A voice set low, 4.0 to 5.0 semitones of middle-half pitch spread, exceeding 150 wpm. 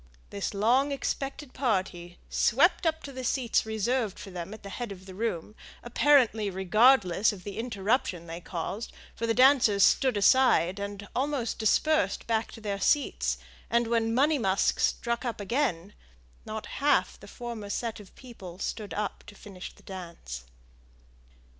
No: high, 220 Hz; average, 4.4 semitones; average, 160 wpm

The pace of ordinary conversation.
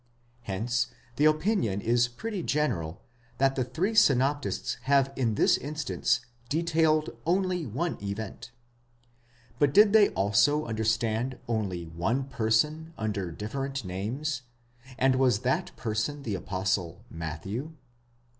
No: slow, 115 wpm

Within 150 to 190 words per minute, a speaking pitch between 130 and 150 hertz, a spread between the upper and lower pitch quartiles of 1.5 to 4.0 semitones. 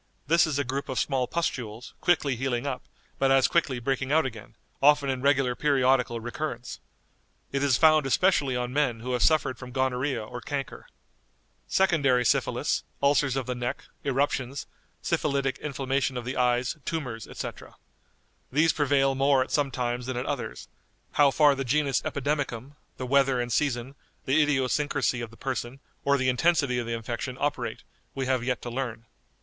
Yes: average, 170 wpm; low, 135 Hz; narrow, 2.4 semitones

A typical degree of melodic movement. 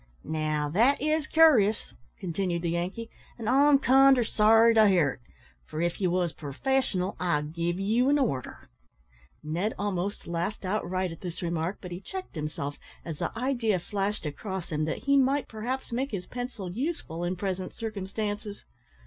No: wide, 5.7 semitones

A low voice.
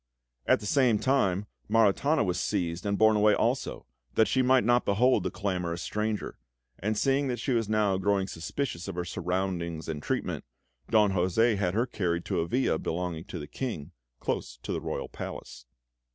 Yes: low, 100 Hz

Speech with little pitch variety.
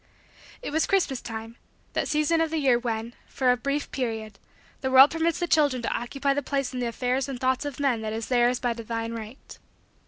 No: average, 3.6 semitones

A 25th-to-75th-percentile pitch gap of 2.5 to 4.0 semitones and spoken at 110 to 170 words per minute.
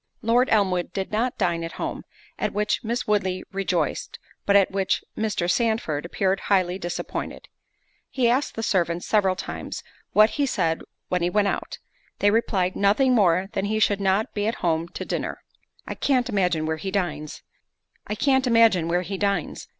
Yes: average, 3.5 semitones; average, 160 wpm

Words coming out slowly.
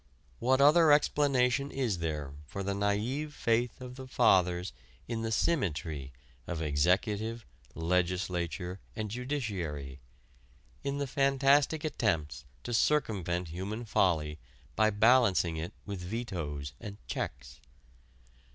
Yes: slow, 115 wpm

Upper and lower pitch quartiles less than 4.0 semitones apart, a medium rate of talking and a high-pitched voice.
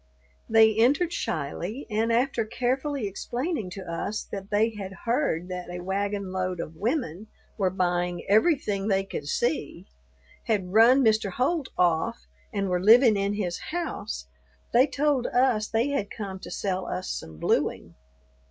No: average, 4.7 semitones; average, 150 wpm; high, 210 Hz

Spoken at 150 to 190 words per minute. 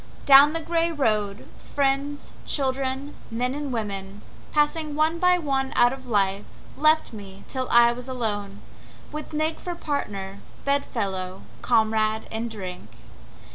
No: slow, 135 wpm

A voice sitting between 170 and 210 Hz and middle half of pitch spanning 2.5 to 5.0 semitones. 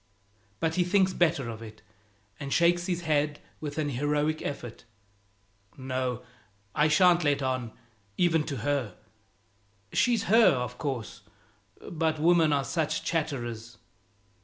No: medium, 145 Hz; average, 4.5 semitones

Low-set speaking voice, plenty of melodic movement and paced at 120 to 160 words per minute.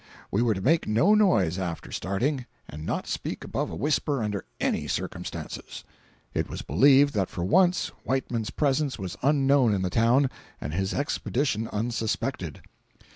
Yes: low, 115 Hz; wide, 6.5 semitones; average, 155 wpm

